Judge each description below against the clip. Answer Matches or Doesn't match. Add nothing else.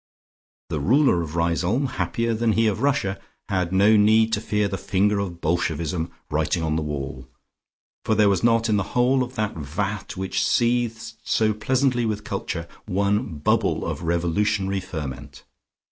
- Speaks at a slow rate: Doesn't match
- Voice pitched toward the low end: Matches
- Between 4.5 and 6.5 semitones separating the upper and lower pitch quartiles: Matches